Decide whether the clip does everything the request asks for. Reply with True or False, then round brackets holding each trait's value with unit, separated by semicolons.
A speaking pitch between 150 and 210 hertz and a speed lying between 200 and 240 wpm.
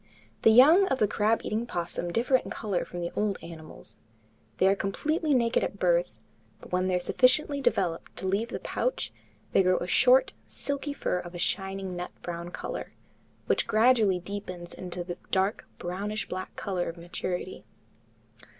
False (190 Hz; 170 wpm)